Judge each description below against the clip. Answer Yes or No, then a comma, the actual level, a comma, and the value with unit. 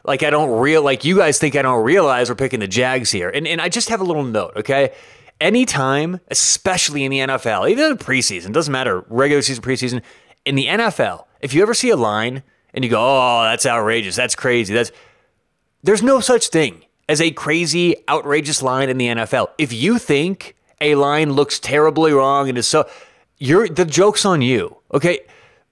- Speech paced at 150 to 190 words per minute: No, average, 200 wpm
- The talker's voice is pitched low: No, medium, 145 Hz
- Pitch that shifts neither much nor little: No, wide, 5.8 semitones